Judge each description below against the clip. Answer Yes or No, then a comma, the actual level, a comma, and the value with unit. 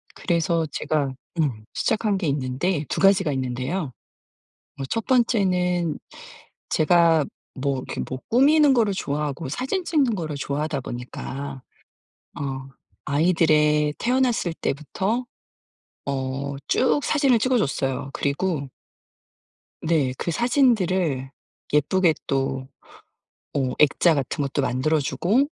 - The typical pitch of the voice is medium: Yes, medium, 155 Hz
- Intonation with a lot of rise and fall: Yes, wide, 6.0 semitones